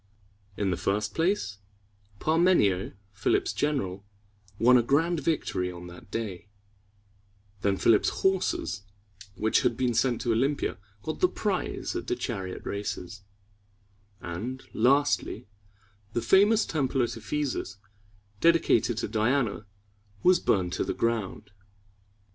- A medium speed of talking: No, slow, 125 wpm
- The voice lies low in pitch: Yes, low, 115 Hz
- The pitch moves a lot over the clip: Yes, wide, 6.8 semitones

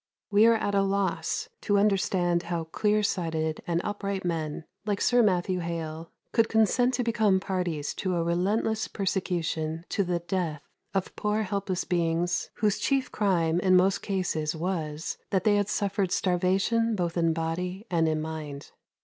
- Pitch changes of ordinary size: Yes, average, 3.5 semitones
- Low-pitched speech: No, medium, 185 Hz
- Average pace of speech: Yes, average, 160 wpm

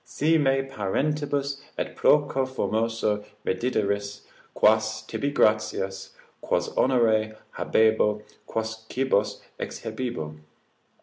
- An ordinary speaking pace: No, slow, 85 wpm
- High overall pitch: No, low, 110 Hz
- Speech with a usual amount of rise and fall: Yes, average, 4.0 semitones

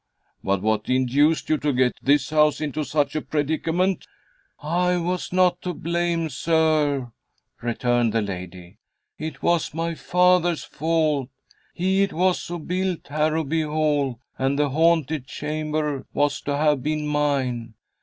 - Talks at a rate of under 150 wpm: Yes, average, 140 wpm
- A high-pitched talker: No, medium, 150 Hz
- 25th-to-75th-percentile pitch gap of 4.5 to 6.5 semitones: No, average, 3.4 semitones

